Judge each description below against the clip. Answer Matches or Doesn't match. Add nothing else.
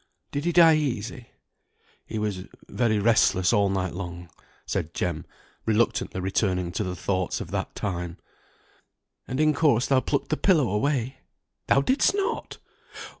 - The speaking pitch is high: Doesn't match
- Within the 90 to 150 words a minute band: Matches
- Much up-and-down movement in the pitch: Matches